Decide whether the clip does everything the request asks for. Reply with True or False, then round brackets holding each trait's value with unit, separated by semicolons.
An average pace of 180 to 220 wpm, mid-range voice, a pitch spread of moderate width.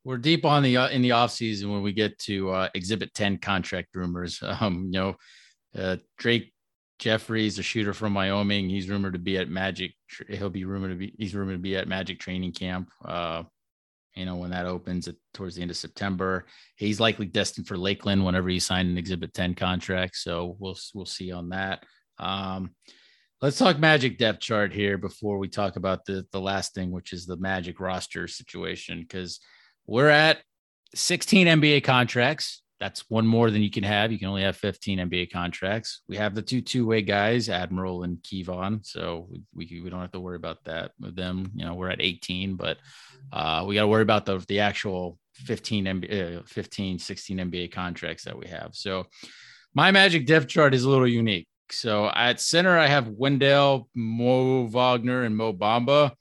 False (195 wpm; 100 Hz; 3.7 semitones)